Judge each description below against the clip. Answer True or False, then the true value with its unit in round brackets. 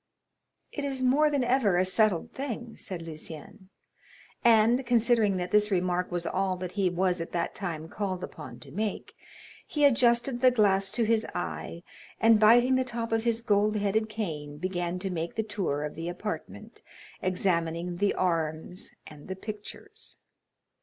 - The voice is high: True (200 Hz)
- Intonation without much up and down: False (4.6 semitones)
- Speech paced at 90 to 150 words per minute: False (160 wpm)